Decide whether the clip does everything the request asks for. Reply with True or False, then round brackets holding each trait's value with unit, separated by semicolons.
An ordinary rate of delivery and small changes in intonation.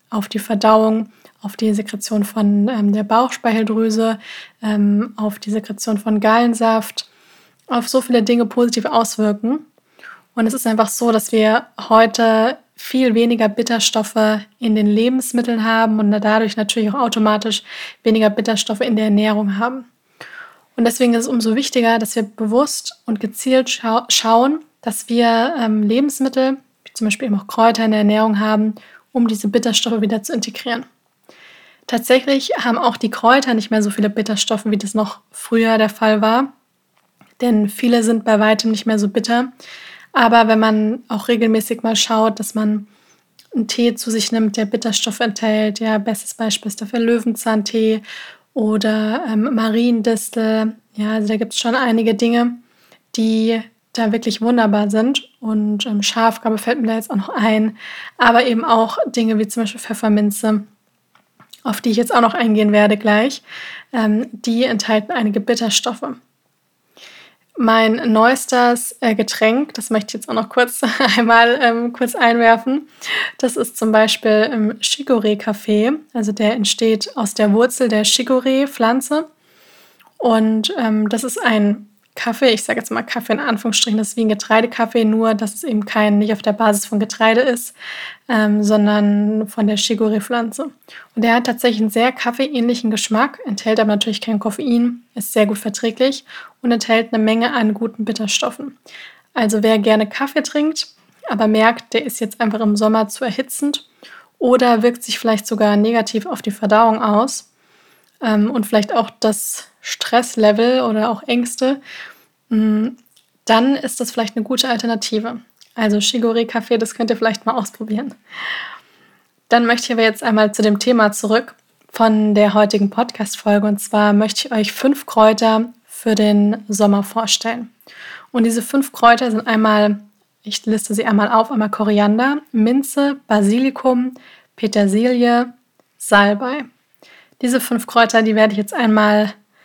True (155 wpm; 1.7 semitones)